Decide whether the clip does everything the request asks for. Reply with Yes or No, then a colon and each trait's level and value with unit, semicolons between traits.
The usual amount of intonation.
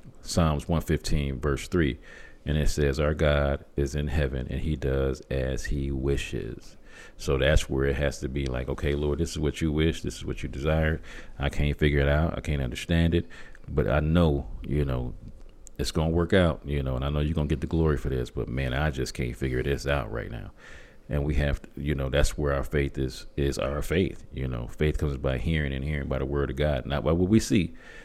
No: narrow, 2.3 semitones